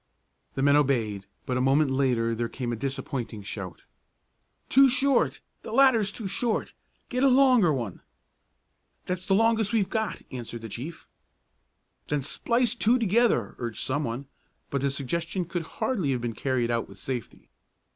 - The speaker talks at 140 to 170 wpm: Yes, average, 160 wpm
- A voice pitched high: No, medium, 140 Hz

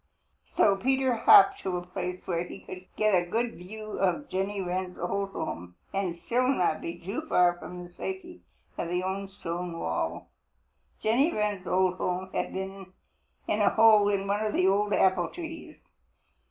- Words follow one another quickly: No, average, 175 wpm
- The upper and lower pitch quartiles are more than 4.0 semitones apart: No, average, 3.2 semitones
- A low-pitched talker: No, high, 190 Hz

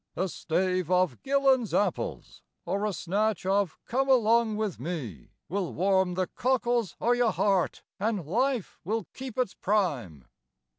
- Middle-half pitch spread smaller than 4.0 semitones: No, average, 4.4 semitones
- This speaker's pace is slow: No, average, 145 wpm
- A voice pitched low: No, high, 200 Hz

